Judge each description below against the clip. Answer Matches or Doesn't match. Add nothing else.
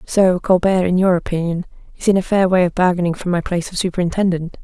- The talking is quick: Matches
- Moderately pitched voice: Matches